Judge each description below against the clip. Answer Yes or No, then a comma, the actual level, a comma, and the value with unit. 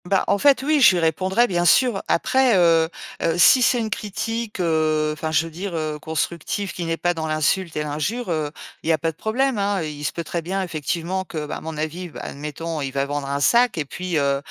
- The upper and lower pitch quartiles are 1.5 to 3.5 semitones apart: No, average, 4.3 semitones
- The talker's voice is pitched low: No, medium, 170 Hz